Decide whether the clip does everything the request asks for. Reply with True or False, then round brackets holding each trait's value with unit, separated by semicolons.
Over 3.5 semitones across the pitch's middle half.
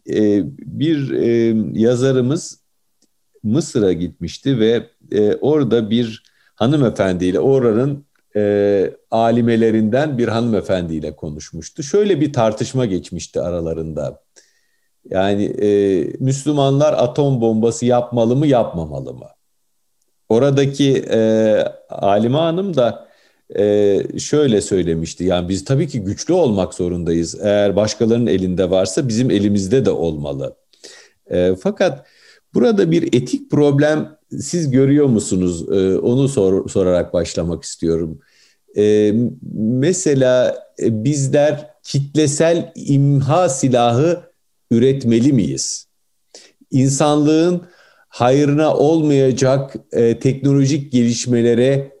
True (5.6 semitones)